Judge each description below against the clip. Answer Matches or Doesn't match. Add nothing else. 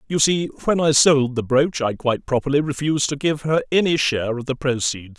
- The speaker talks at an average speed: Doesn't match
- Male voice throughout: Matches